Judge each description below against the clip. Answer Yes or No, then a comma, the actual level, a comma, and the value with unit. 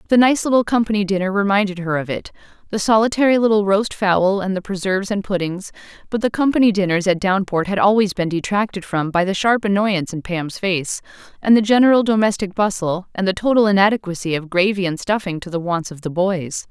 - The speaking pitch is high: Yes, high, 195 Hz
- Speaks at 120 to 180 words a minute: No, average, 200 wpm